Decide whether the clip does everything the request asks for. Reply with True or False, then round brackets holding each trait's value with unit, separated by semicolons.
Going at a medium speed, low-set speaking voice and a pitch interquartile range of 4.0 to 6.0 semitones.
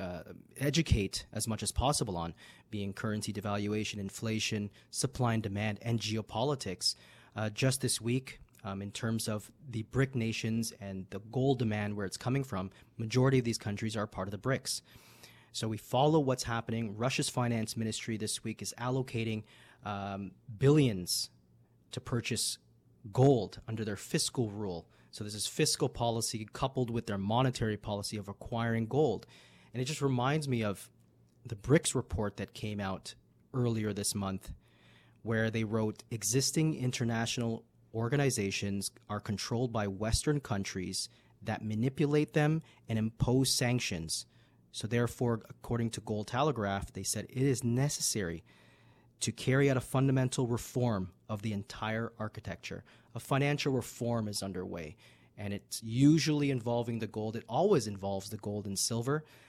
False (150 wpm; 115 Hz; 3.5 semitones)